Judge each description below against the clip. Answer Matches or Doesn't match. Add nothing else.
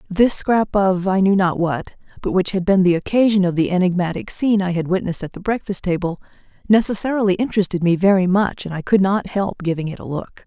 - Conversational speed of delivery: Doesn't match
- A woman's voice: Matches